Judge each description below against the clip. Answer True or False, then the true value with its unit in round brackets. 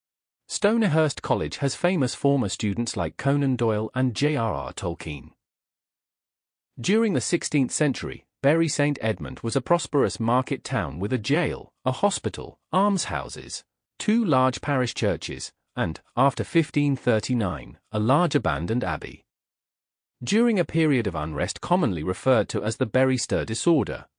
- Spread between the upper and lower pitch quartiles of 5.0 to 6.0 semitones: True (5.4 semitones)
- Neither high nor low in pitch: False (130 Hz)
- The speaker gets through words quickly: False (140 wpm)